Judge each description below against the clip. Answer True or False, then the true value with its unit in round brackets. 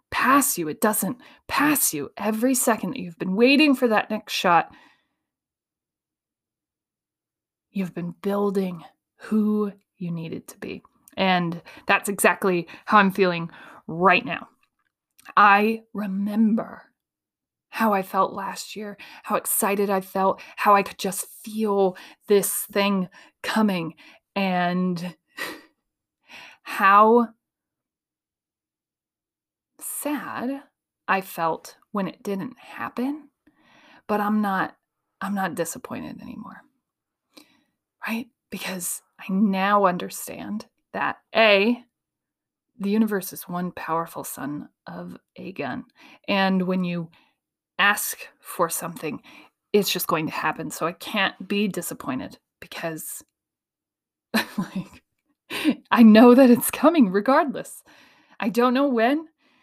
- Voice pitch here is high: True (205 Hz)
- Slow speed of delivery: True (110 wpm)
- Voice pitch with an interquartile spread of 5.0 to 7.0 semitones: False (4.1 semitones)